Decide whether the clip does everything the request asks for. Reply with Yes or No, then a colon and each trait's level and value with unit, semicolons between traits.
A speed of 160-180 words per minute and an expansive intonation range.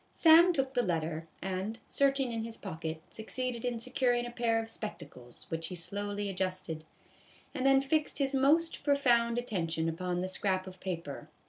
Yes: average, 165 wpm; wide, 6.2 semitones